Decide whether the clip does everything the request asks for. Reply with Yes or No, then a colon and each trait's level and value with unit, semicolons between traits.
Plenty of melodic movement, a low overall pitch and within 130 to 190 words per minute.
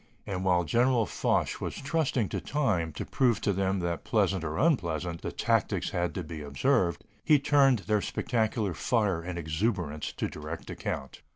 Yes: wide, 6.2 semitones; very low, 95 Hz; average, 170 wpm